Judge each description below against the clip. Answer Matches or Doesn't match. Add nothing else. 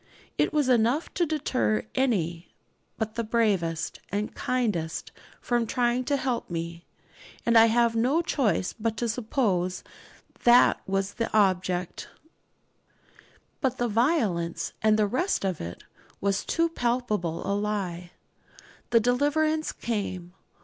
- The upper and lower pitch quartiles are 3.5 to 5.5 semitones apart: Matches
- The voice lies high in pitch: Matches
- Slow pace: Matches